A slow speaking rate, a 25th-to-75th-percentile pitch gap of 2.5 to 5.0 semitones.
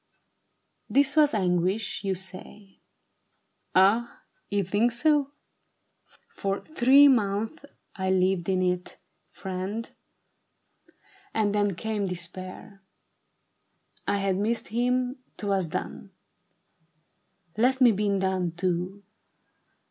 Yes: slow, 100 wpm; average, 4.0 semitones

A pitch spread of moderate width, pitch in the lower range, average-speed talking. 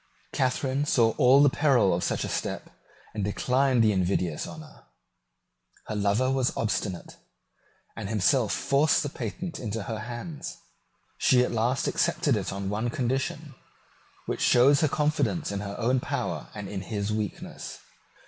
Yes: average, 4.6 semitones; low, 120 Hz; average, 150 wpm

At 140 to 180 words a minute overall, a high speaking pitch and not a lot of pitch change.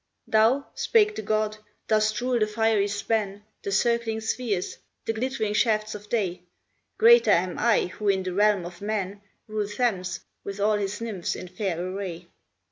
Yes: average, 165 wpm; high, 210 Hz; narrow, 2.3 semitones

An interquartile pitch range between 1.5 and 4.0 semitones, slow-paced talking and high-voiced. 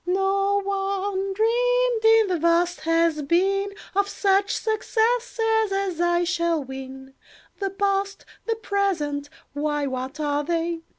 Yes: average, 3.7 semitones; slow, 120 wpm; very high, 385 Hz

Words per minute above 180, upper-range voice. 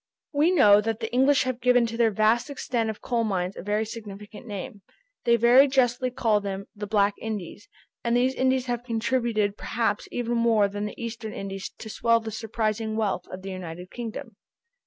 Yes: average, 190 wpm; high, 225 Hz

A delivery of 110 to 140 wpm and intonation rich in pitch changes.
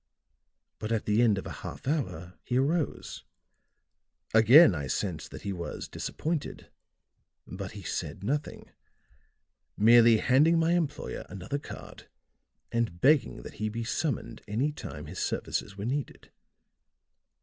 Yes: slow, 135 wpm; wide, 6.3 semitones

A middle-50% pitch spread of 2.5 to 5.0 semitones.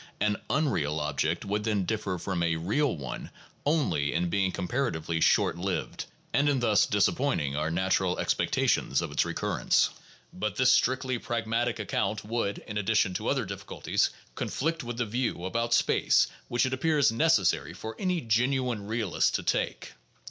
No: wide, 5.6 semitones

